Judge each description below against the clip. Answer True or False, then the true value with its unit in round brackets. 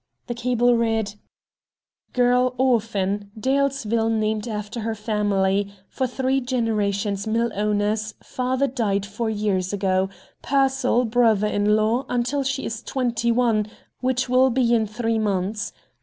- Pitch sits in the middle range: False (225 Hz)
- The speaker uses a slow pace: True (130 wpm)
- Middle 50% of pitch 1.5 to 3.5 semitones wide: True (3.2 semitones)